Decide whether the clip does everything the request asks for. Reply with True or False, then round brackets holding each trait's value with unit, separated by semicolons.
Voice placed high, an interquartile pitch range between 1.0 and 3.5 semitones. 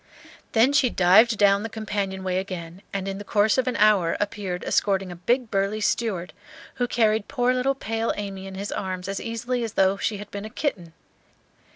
True (205 Hz; 2.9 semitones)